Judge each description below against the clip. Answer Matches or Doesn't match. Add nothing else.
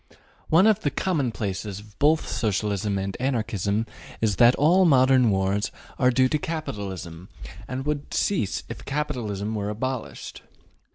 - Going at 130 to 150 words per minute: Matches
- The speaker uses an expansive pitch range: Matches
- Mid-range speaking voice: Doesn't match